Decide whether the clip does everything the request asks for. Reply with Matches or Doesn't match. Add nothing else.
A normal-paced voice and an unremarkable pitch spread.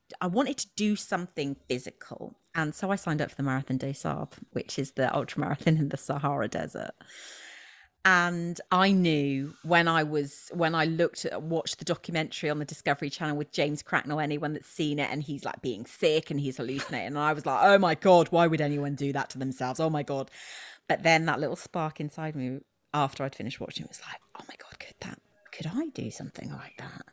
Doesn't match